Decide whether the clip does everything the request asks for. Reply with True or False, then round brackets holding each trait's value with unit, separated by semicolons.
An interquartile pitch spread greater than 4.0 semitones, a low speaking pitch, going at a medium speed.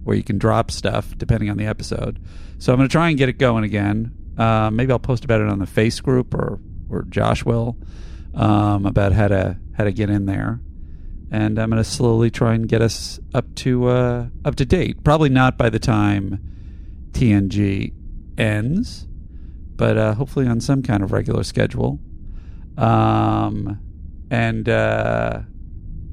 True (4.8 semitones; 105 Hz; 175 wpm)